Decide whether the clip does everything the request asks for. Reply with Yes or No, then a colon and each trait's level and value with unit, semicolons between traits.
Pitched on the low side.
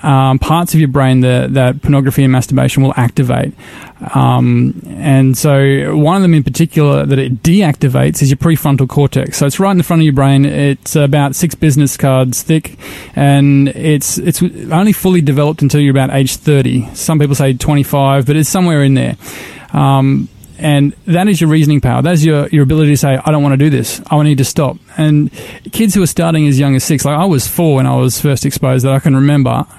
No: medium, 145 Hz